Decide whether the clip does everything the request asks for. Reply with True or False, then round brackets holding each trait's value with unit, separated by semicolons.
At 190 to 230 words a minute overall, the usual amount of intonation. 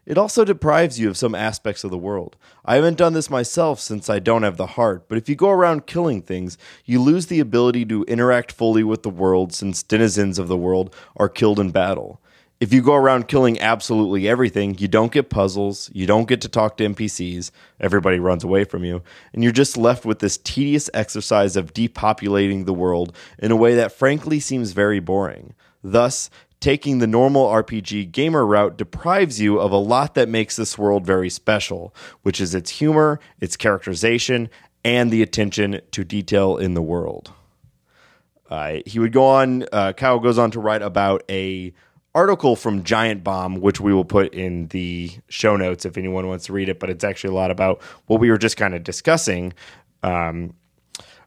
True (195 wpm; 4.2 semitones)